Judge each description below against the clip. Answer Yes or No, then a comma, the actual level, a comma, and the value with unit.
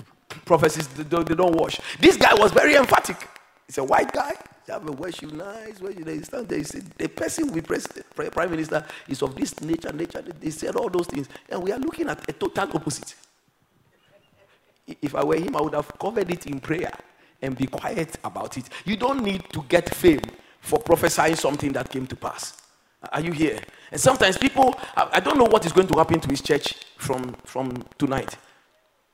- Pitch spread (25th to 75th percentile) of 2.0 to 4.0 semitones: No, wide, 5.5 semitones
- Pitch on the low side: No, medium, 165 Hz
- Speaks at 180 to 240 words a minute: Yes, average, 200 wpm